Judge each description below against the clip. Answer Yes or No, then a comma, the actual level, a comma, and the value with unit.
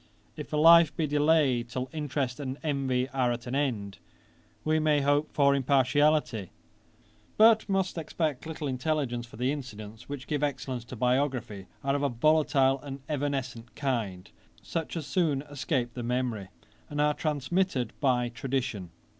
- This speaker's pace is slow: No, average, 155 wpm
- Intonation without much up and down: No, average, 3.4 semitones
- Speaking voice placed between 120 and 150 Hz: Yes, low, 135 Hz